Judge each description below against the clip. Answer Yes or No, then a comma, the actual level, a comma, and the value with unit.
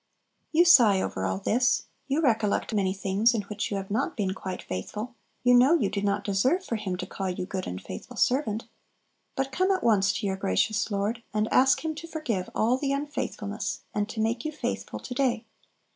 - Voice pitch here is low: No, high, 220 Hz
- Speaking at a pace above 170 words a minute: Yes, fast, 205 wpm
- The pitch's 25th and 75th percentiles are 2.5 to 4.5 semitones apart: No, average, 4.9 semitones